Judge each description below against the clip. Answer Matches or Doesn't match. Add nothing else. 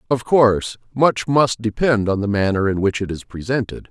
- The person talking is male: Matches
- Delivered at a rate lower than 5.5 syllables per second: Matches